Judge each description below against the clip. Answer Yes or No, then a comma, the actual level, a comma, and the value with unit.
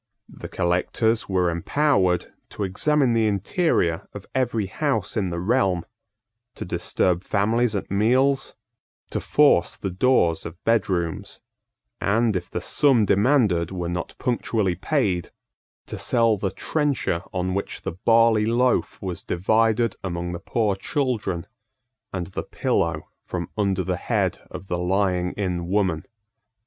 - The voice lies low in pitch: Yes, low, 100 Hz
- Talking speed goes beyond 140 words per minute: No, slow, 135 wpm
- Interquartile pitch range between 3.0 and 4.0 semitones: No, average, 4.5 semitones